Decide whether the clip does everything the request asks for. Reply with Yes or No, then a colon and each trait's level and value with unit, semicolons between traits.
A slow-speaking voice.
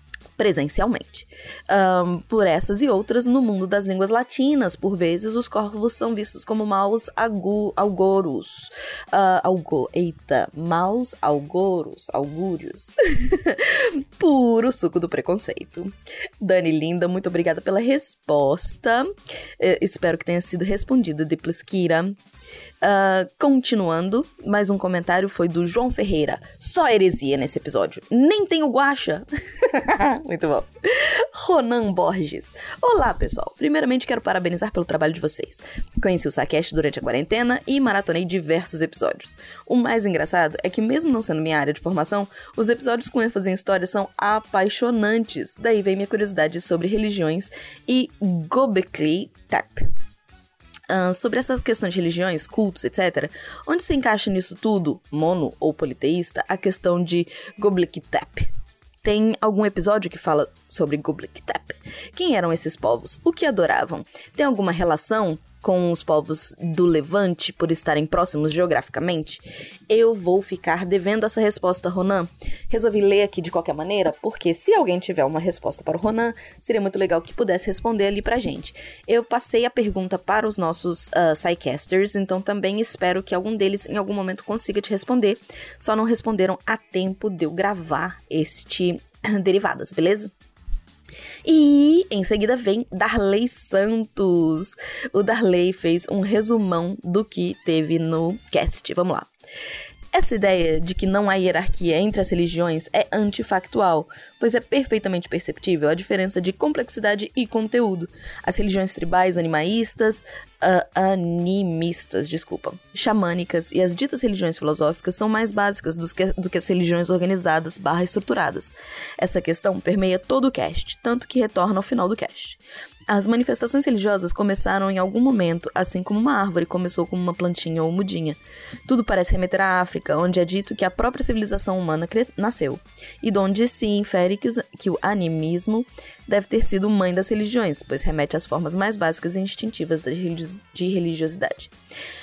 No: average, 150 wpm